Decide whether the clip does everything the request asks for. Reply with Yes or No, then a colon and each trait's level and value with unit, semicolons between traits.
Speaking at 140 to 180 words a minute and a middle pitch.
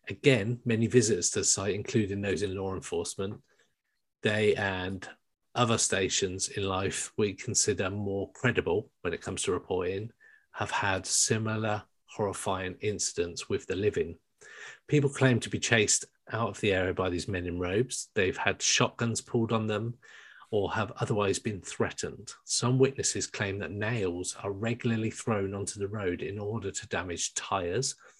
No: average, 160 wpm; low, 105 Hz